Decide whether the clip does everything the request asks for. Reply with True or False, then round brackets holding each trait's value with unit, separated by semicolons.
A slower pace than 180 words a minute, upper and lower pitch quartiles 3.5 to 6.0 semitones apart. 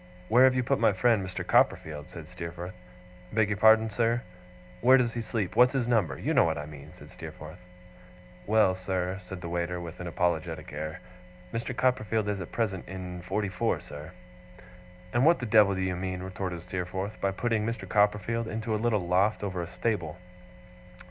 False (190 wpm; 4.1 semitones)